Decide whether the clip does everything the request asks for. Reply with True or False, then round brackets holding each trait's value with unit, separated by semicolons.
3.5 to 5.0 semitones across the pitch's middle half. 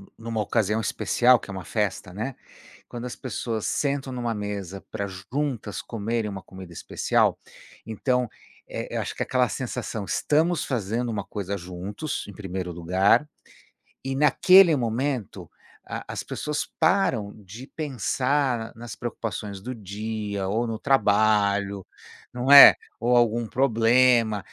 True (3.9 semitones)